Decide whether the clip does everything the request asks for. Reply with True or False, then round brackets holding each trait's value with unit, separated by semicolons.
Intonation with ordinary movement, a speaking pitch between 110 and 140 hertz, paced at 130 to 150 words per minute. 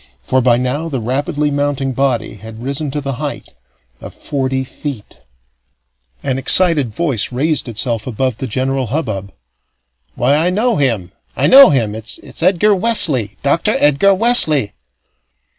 True (4.1 semitones; 135 Hz; 140 wpm)